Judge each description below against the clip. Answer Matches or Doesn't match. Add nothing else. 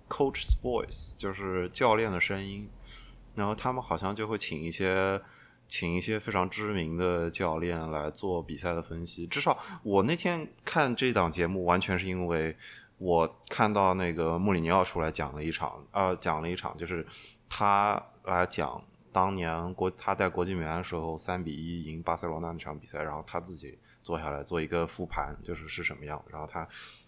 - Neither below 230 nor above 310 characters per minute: Matches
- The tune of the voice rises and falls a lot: Doesn't match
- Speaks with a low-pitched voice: Matches